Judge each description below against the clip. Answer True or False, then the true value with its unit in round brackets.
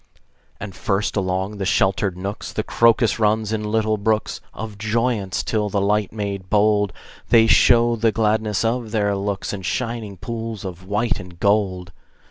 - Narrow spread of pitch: True (2.2 semitones)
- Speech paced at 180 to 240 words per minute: False (160 wpm)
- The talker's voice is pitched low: True (105 Hz)